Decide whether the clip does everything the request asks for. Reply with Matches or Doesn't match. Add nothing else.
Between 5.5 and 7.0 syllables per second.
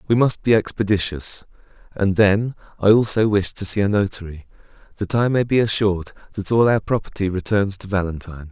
Matches